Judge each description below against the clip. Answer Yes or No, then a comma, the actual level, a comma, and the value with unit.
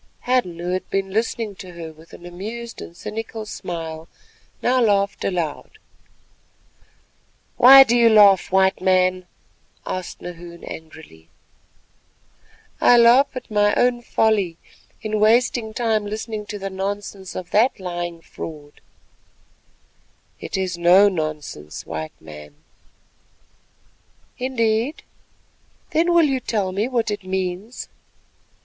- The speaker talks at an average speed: No, slow, 120 wpm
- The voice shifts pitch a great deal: No, average, 4.5 semitones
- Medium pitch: No, high, 195 Hz